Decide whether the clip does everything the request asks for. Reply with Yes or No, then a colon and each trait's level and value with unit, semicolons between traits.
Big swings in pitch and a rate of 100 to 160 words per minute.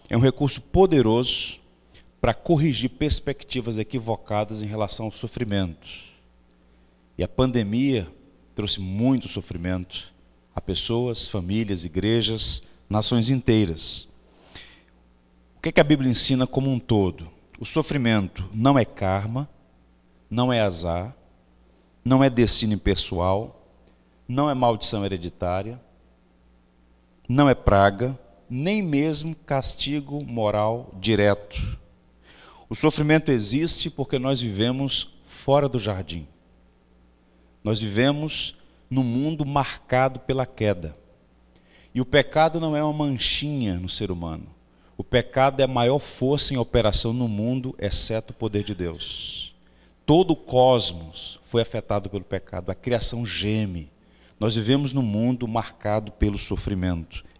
Yes: wide, 6.8 semitones; slow, 120 wpm